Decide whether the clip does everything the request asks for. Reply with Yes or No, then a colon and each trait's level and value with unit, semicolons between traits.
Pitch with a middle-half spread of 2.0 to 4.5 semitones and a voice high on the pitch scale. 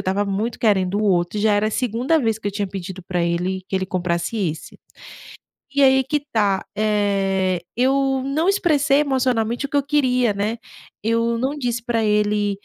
No: average, 4.9 semitones; high, 215 Hz